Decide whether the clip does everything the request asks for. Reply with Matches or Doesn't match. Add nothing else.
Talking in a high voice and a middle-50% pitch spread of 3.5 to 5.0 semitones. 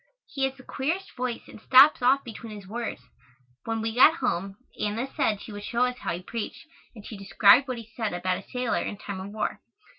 Matches